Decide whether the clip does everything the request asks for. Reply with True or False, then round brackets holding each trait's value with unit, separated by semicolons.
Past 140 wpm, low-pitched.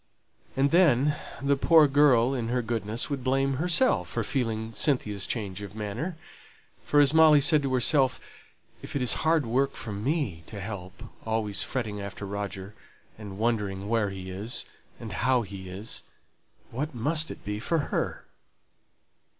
True (160 wpm; 120 Hz)